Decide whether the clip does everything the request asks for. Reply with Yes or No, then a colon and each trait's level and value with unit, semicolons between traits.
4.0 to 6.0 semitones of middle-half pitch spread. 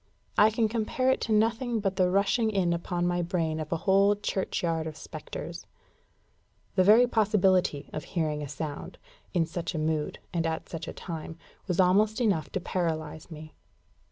Yes: average, 4.4 semitones